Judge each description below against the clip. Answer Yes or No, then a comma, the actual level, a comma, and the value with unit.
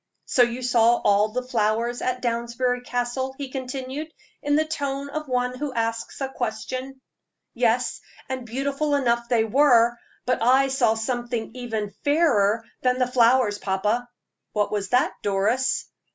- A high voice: Yes, high, 245 Hz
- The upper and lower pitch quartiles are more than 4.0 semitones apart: No, narrow, 2.4 semitones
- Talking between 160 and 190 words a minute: No, average, 150 wpm